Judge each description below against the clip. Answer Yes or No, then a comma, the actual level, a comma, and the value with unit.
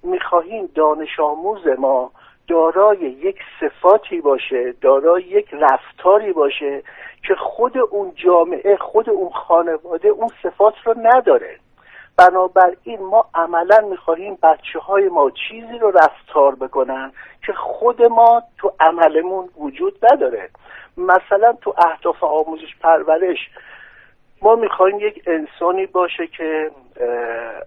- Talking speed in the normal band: Yes, average, 115 wpm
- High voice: Yes, high, 195 Hz